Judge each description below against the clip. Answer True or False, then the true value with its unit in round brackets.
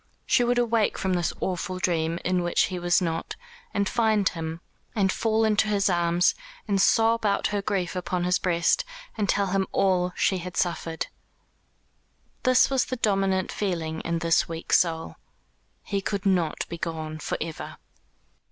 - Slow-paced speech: False (165 wpm)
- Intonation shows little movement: False (3.2 semitones)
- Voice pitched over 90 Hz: True (185 Hz)